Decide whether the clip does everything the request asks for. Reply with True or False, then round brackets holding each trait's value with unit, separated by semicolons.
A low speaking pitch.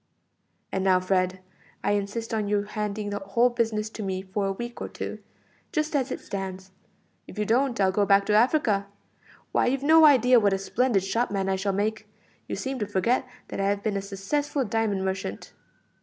False (205 Hz)